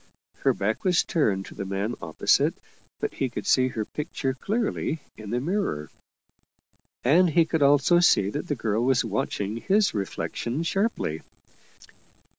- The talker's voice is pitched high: No, low, 130 Hz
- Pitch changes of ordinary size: No, wide, 8.0 semitones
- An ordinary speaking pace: Yes, average, 155 wpm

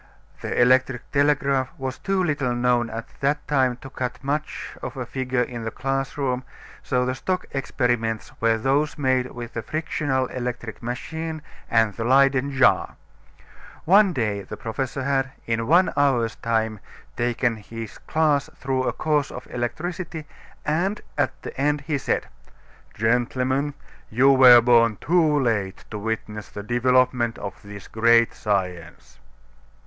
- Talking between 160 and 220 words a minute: No, average, 145 wpm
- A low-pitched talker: Yes, low, 130 Hz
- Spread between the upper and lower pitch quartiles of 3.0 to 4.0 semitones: Yes, average, 3.4 semitones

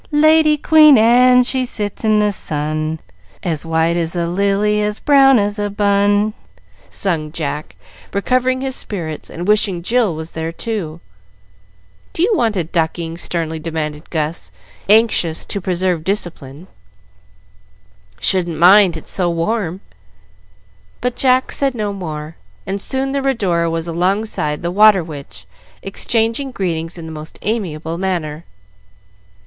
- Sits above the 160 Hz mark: Yes, high, 190 Hz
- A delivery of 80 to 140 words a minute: Yes, slow, 135 wpm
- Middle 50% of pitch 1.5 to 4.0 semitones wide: No, average, 5.2 semitones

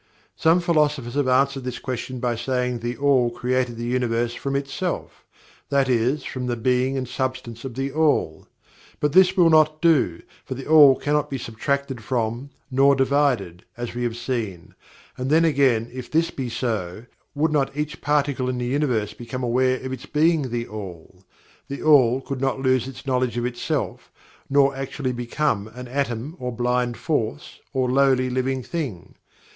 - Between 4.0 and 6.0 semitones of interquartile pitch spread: No, average, 2.7 semitones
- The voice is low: Yes, low, 130 Hz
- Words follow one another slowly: No, average, 175 wpm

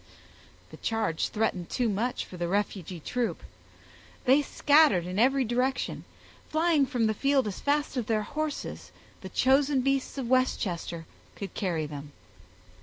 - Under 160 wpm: Yes, average, 145 wpm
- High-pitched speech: Yes, high, 240 Hz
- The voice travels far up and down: Yes, wide, 6.4 semitones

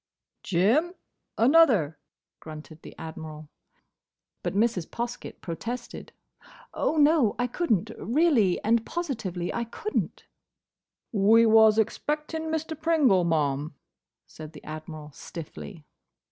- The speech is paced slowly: Yes, slow, 110 wpm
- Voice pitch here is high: Yes, high, 220 Hz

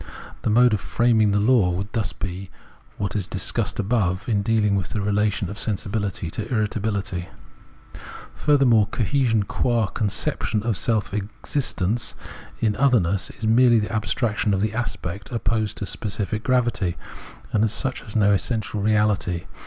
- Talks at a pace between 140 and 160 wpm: Yes, average, 155 wpm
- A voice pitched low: Yes, low, 105 Hz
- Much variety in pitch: No, narrow, 2.4 semitones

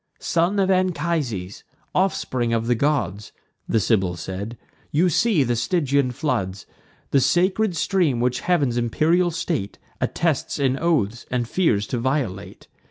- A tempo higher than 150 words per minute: No, slow, 135 wpm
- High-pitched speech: No, low, 135 Hz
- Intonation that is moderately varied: No, wide, 6.9 semitones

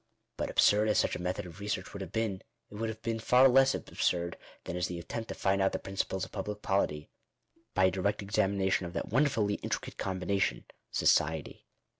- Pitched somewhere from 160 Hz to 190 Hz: No, low, 100 Hz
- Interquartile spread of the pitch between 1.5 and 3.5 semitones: Yes, average, 3.0 semitones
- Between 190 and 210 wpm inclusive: Yes, fast, 205 wpm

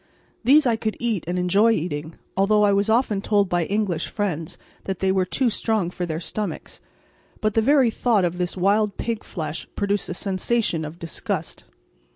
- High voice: Yes, high, 200 Hz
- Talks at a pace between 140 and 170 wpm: No, average, 185 wpm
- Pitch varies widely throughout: No, average, 3.7 semitones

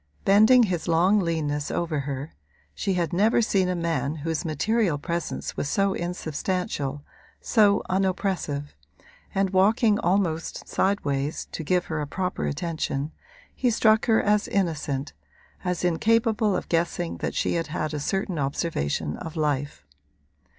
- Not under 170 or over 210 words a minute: No, average, 140 wpm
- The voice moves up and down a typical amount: Yes, average, 4.7 semitones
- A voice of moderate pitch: Yes, medium, 175 Hz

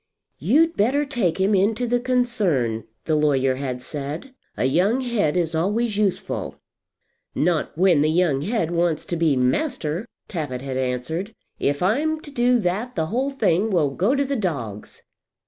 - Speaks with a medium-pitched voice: Yes, medium, 180 Hz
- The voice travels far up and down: Yes, wide, 8.2 semitones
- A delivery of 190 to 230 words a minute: No, average, 165 wpm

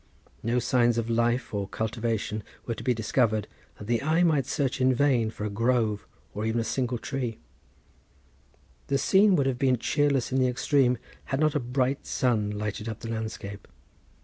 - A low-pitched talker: Yes, low, 120 Hz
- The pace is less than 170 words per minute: No, average, 180 wpm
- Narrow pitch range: No, average, 3.2 semitones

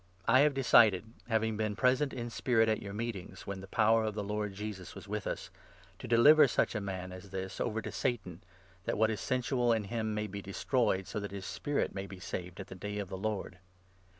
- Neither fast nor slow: No, fast, 240 wpm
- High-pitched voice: No, low, 105 Hz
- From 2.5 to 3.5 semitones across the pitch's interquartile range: Yes, average, 3.2 semitones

